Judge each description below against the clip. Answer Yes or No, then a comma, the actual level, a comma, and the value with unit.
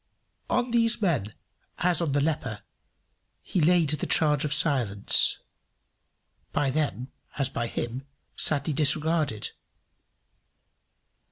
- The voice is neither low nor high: Yes, medium, 150 Hz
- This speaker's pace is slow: Yes, slow, 105 wpm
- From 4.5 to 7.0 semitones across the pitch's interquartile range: No, average, 3.8 semitones